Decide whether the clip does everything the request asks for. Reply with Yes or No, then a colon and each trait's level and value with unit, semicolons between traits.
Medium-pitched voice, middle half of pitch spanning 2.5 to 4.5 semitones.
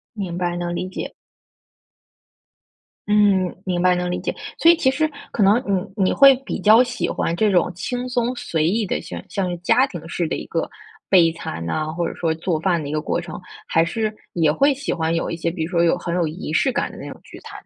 Yes: medium, 180 Hz; average, 4.1 semitones